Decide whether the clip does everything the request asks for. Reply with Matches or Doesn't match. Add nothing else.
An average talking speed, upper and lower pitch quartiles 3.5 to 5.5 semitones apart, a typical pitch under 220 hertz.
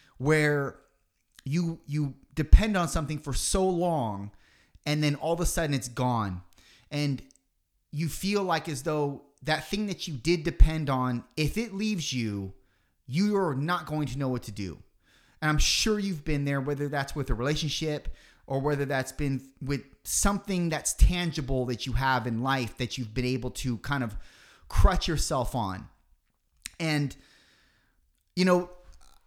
Matches